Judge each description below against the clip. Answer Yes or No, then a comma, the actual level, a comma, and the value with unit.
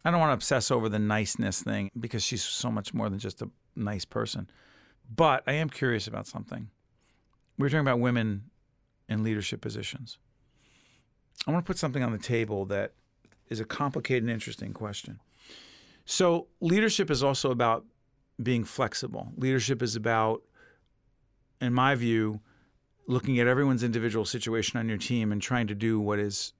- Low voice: Yes, low, 120 Hz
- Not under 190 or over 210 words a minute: No, average, 170 wpm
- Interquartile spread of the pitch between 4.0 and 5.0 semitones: No, average, 3.1 semitones